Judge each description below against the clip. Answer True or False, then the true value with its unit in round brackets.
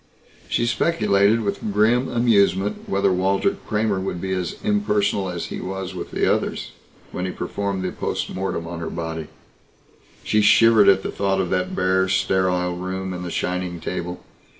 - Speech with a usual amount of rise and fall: False (2.1 semitones)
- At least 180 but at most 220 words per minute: False (170 wpm)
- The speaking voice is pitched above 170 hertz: False (95 Hz)